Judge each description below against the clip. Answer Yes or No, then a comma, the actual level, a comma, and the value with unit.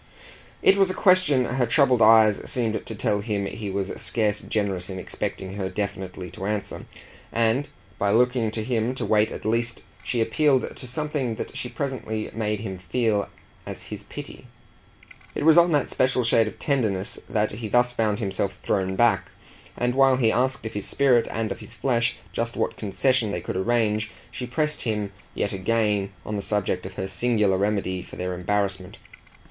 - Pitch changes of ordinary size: Yes, average, 3.6 semitones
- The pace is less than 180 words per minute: No, average, 185 wpm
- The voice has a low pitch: Yes, low, 110 Hz